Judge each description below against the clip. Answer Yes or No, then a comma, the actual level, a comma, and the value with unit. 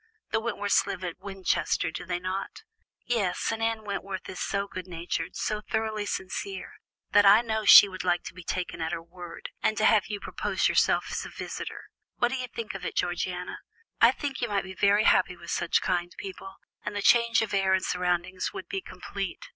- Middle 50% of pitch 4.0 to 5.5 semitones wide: No, average, 3.3 semitones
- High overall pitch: Yes, high, 195 Hz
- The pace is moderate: No, fast, 210 wpm